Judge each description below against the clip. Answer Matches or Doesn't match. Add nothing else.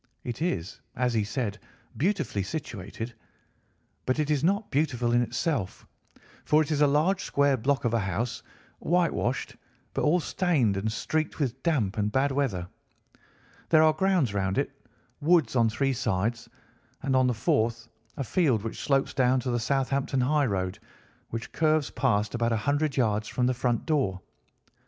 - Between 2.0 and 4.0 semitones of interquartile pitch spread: Doesn't match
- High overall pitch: Doesn't match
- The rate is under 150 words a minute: Doesn't match